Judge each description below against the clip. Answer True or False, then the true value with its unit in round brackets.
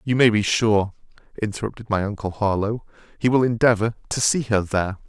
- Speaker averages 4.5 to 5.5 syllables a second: False (6.0 syllables/s)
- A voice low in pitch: True (110 Hz)